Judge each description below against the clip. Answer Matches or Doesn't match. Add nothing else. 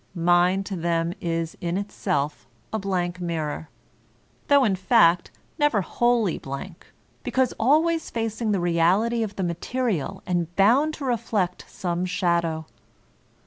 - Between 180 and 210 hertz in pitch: Matches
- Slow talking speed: Matches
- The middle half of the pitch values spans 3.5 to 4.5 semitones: Doesn't match